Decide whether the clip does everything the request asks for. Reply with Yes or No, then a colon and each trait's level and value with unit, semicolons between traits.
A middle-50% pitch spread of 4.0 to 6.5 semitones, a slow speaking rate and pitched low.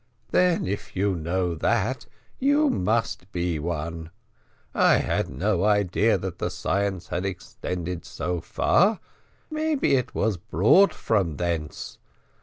Yes: average, 4.6 semitones; slow, 125 wpm; very low, 95 Hz